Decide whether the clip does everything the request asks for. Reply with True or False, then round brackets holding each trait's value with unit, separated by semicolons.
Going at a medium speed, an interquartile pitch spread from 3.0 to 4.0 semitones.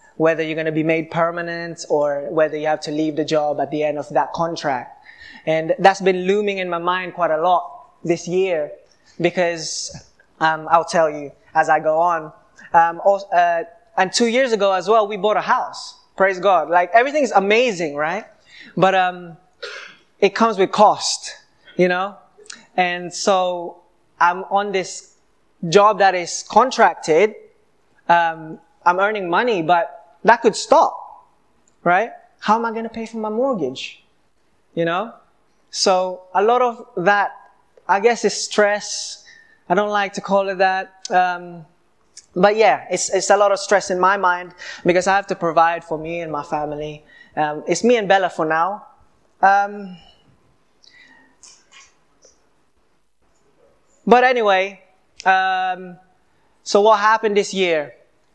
True (155 wpm; 3.5 semitones)